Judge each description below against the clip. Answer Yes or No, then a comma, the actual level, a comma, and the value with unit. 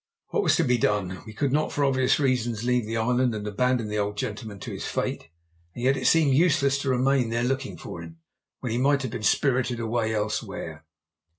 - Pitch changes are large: No, average, 3.6 semitones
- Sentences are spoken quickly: Yes, fast, 215 wpm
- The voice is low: Yes, low, 125 Hz